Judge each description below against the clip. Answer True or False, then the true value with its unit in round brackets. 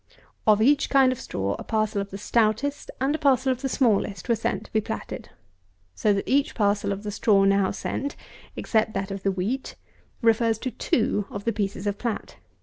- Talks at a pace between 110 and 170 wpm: False (205 wpm)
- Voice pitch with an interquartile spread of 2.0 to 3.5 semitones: False (4.3 semitones)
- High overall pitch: True (215 Hz)